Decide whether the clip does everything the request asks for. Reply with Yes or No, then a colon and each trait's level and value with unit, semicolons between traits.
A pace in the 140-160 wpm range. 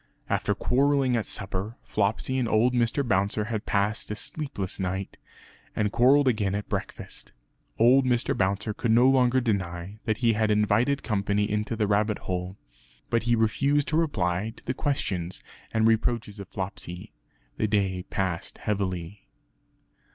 Yes: average, 150 wpm